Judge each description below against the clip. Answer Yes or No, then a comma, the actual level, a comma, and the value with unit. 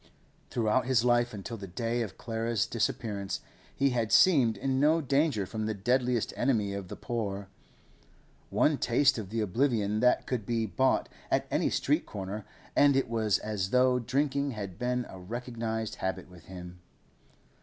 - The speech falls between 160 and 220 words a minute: Yes, average, 165 wpm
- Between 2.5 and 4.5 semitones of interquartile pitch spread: Yes, average, 3.7 semitones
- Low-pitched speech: Yes, low, 115 Hz